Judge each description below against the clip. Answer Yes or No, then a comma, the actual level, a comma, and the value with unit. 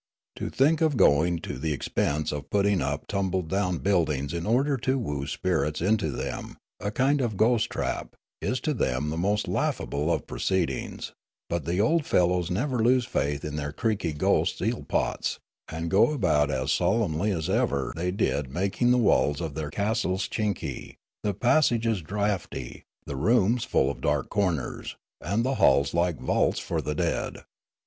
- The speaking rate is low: No, average, 170 wpm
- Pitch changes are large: Yes, wide, 6.8 semitones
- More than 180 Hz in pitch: No, very low, 95 Hz